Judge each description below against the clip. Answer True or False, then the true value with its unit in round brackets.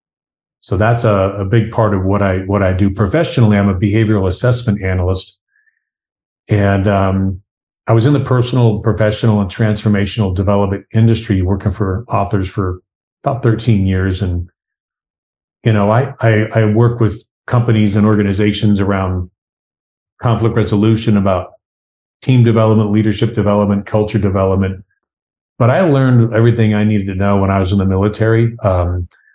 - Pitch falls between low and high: False (105 Hz)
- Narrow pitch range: True (2.3 semitones)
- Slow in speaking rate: False (150 wpm)